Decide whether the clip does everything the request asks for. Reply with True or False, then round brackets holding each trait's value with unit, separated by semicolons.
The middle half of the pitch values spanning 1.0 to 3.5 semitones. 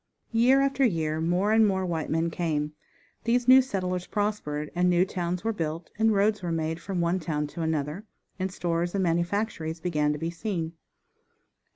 False (4.0 semitones)